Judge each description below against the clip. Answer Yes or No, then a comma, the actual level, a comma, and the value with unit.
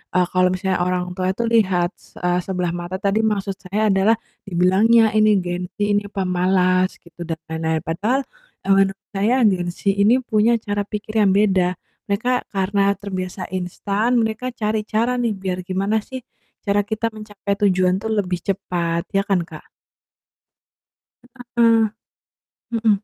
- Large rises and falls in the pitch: No, average, 2.8 semitones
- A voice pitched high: Yes, high, 195 Hz